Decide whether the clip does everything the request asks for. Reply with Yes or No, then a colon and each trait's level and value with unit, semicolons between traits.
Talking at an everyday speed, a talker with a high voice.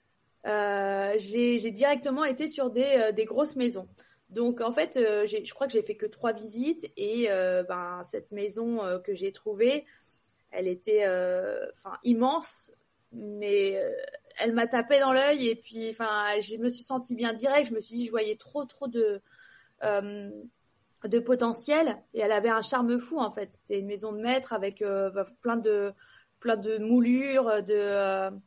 Yes: average, 185 wpm; high, 230 Hz